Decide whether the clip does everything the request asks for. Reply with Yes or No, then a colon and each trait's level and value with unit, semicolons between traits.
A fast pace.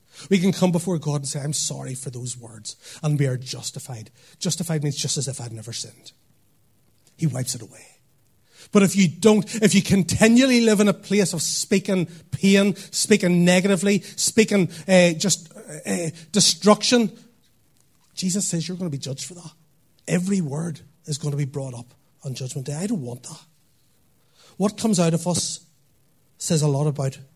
No: average, 180 wpm